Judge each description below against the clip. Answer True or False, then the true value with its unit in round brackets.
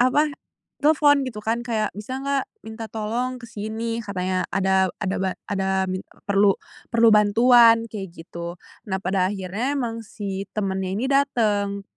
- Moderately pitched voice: False (215 Hz)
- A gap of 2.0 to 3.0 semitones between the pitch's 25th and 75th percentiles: False (3.5 semitones)